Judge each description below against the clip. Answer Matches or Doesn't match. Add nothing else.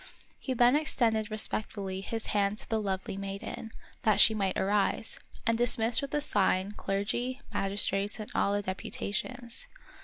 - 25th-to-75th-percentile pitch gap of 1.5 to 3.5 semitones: Matches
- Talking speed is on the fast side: Doesn't match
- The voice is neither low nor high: Doesn't match